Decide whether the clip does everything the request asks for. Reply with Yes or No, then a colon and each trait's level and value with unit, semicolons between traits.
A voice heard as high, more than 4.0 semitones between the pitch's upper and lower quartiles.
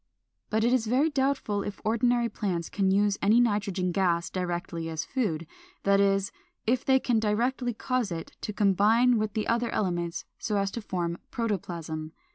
Yes: high, 205 Hz; average, 4.4 semitones